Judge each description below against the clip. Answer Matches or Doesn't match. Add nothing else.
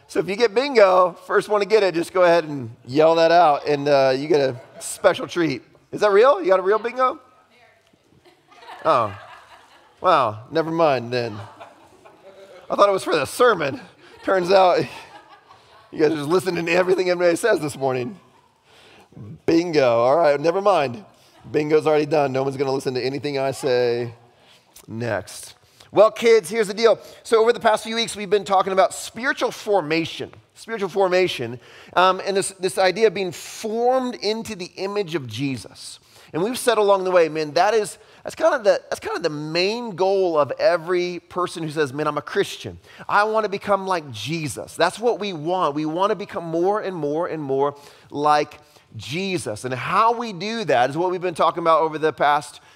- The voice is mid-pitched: Matches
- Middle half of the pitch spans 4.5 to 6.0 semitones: Matches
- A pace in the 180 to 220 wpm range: Matches